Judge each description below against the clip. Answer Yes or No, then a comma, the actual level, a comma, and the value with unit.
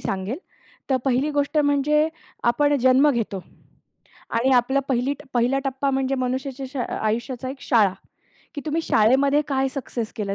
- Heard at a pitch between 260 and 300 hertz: Yes, very high, 265 Hz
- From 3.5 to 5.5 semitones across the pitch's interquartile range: No, average, 2.9 semitones